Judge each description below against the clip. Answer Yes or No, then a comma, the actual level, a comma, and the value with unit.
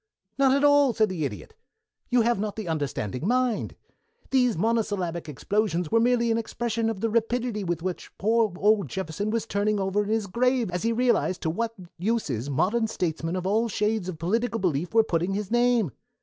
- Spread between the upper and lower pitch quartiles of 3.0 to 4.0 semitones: No, average, 4.5 semitones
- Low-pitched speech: No, high, 215 Hz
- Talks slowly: No, average, 190 wpm